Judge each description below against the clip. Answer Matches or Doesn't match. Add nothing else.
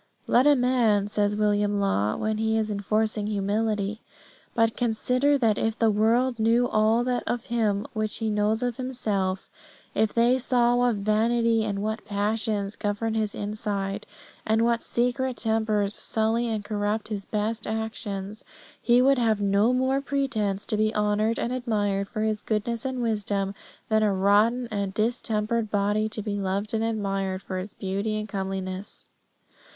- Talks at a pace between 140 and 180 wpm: Matches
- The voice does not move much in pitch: Matches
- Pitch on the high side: Matches